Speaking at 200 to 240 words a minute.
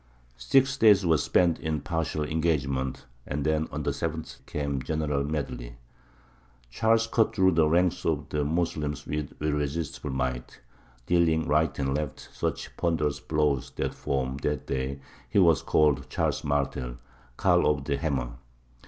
No: average, 150 wpm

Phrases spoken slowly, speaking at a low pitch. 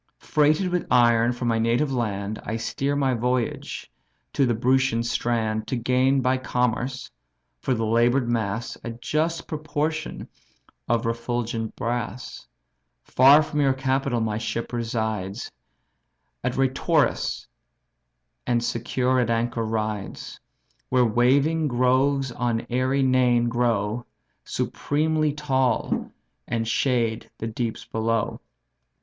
Yes: slow, 120 wpm; low, 120 Hz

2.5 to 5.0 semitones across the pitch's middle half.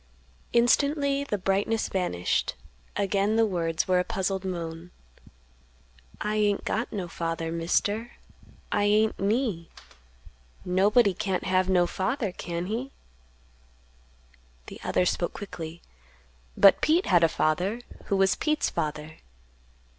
Yes: average, 4.0 semitones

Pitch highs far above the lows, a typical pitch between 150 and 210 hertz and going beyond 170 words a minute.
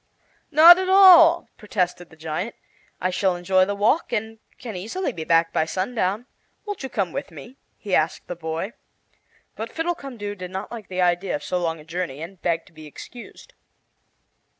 Yes: wide, 6.2 semitones; high, 190 Hz; average, 180 wpm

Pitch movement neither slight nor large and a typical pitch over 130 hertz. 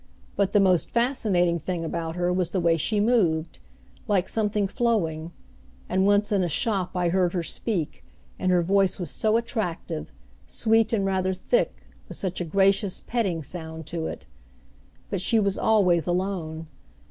Yes: average, 3.3 semitones; medium, 185 Hz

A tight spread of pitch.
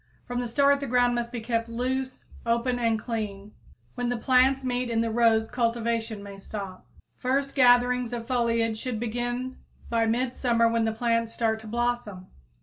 Yes: narrow, 1.6 semitones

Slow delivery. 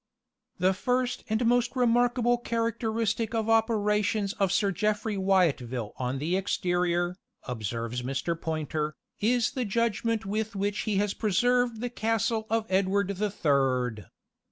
Yes: slow, 130 wpm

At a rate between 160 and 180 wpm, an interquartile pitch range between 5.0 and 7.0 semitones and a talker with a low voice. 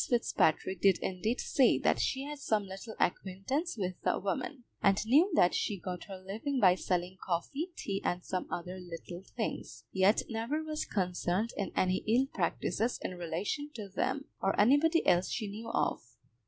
No: average, 170 wpm; wide, 5.4 semitones; high, 200 Hz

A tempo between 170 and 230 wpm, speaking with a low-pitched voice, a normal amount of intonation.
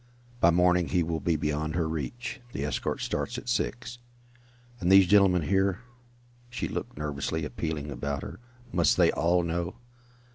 No: average, 160 wpm; very low, 85 Hz; average, 4.1 semitones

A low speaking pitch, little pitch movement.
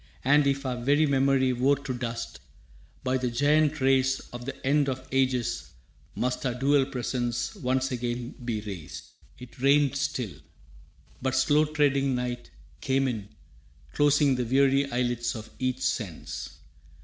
Yes: low, 130 Hz; narrow, 2.2 semitones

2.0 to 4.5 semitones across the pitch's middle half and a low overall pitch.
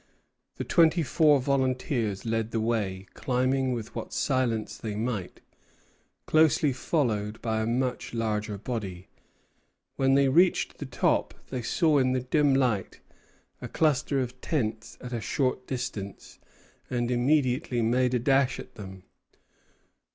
Yes: average, 3.4 semitones; low, 125 Hz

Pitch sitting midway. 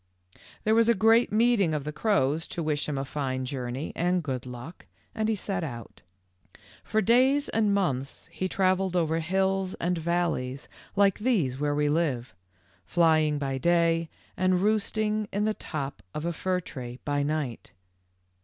Yes: medium, 170 Hz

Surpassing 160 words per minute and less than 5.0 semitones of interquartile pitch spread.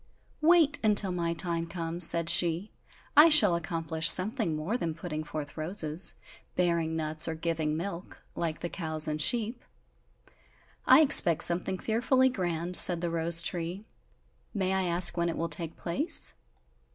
No: average, 150 wpm; average, 2.9 semitones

